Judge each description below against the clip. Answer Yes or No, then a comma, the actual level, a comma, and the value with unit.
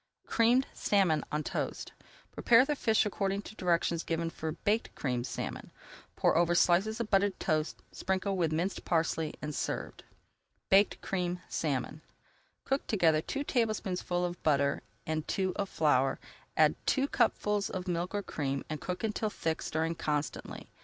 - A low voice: No, medium, 180 Hz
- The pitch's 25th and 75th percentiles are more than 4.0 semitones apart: Yes, average, 4.4 semitones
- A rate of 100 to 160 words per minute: Yes, average, 155 wpm